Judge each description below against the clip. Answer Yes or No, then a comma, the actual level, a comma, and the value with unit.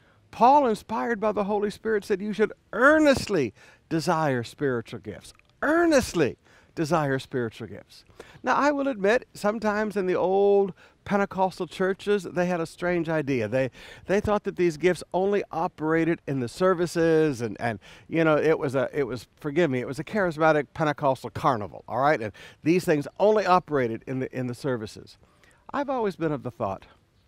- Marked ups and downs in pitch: Yes, wide, 7.4 semitones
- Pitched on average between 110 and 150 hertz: No, medium, 165 Hz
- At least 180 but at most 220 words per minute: No, average, 170 wpm